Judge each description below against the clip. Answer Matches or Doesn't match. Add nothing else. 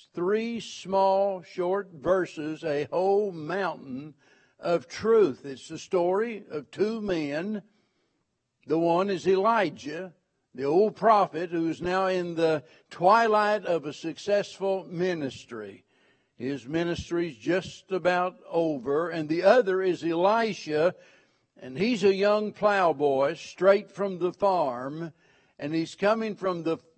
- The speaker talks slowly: Matches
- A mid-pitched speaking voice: Matches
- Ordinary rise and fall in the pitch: Matches